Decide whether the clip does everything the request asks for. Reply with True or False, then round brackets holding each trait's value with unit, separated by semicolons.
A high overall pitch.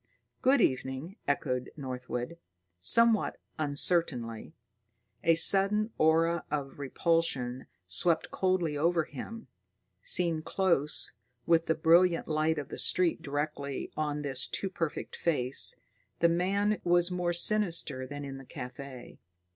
False (160 Hz)